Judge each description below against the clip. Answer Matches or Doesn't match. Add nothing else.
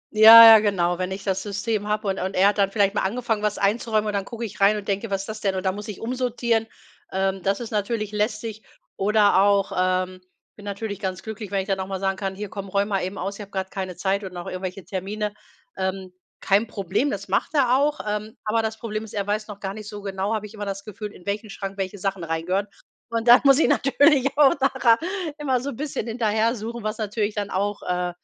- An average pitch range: Doesn't match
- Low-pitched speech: Doesn't match